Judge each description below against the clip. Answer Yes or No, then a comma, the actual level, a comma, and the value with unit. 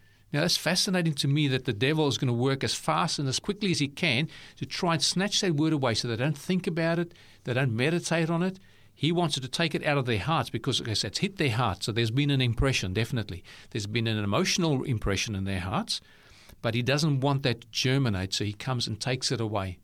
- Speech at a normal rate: No, fast, 250 wpm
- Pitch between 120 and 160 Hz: Yes, low, 135 Hz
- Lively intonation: Yes, wide, 6.0 semitones